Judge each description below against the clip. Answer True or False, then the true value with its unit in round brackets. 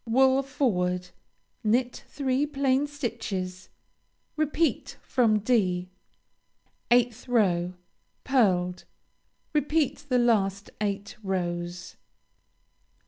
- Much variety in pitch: True (6.3 semitones)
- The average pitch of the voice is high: True (230 Hz)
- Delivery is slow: True (80 wpm)